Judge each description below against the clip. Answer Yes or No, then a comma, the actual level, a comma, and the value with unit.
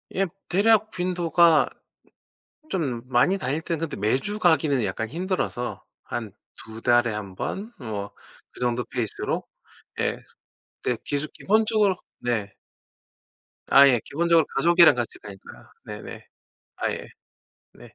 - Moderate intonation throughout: No, wide, 6.9 semitones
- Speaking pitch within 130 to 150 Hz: Yes, medium, 140 Hz